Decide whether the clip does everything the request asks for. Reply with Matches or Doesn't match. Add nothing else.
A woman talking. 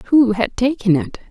Matches